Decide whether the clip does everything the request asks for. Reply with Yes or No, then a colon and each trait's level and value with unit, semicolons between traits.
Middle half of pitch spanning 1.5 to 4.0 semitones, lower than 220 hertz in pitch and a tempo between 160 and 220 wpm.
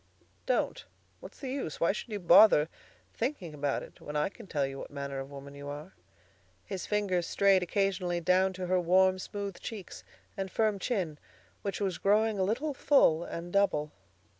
No: average, 4.6 semitones; medium, 185 Hz; average, 180 wpm